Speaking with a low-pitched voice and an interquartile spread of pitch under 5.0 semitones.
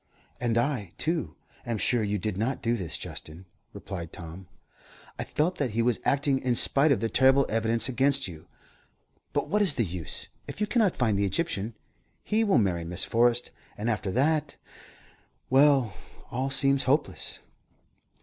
No: low, 120 Hz; wide, 5.4 semitones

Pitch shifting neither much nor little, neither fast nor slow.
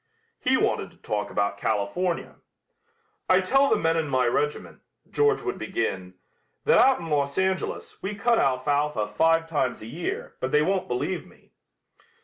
No: wide, 6.8 semitones; average, 160 wpm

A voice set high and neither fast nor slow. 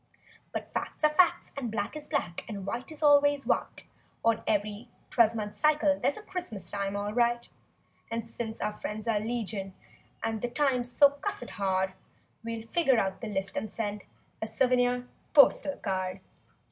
Yes: high, 230 Hz; average, 170 wpm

